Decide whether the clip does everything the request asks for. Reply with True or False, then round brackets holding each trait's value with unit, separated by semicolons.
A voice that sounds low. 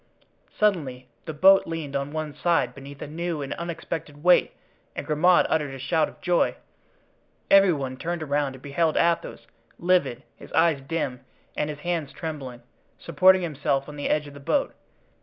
False (150 Hz)